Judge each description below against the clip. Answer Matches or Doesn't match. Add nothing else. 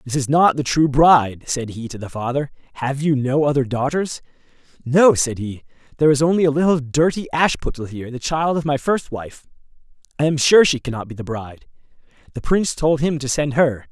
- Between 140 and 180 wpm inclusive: Doesn't match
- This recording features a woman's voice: Doesn't match